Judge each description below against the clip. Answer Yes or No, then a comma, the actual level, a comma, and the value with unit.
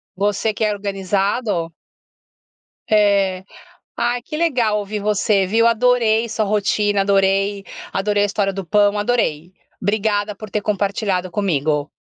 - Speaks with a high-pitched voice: Yes, high, 205 Hz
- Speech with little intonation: Yes, narrow, 1.7 semitones